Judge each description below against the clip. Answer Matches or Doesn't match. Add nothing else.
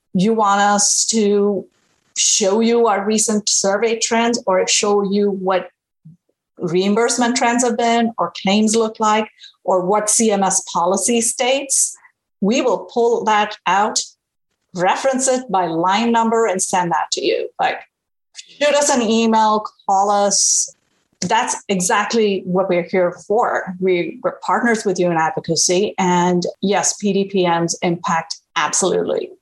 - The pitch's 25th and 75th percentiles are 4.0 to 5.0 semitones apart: Doesn't match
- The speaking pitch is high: Matches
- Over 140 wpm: Doesn't match